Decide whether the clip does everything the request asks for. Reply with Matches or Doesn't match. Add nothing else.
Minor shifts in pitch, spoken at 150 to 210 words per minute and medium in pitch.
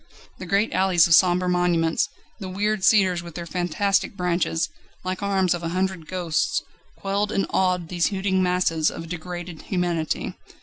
Matches